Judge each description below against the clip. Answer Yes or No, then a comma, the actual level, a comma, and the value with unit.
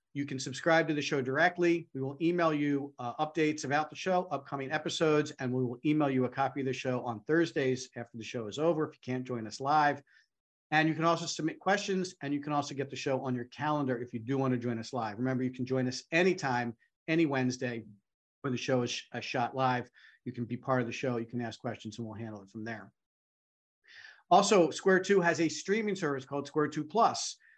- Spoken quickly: Yes, fast, 235 wpm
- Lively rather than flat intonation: No, average, 3.9 semitones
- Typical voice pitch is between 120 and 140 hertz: Yes, low, 135 Hz